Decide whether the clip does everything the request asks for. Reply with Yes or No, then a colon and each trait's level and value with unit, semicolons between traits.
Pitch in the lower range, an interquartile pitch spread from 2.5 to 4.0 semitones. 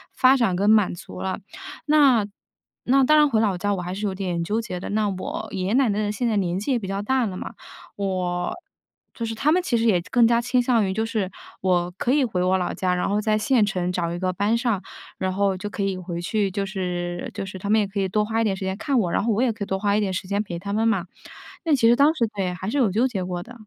No: high, 205 Hz; average, 3.6 semitones